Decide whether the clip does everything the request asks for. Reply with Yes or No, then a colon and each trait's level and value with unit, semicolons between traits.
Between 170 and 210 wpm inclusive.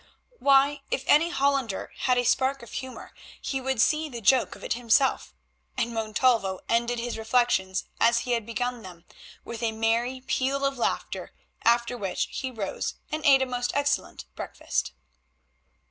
No: average, 160 wpm